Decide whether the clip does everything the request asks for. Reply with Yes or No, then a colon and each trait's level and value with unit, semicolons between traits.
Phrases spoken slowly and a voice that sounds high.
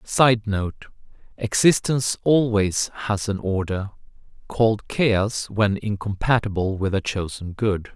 No: slow, 105 wpm; low, 105 Hz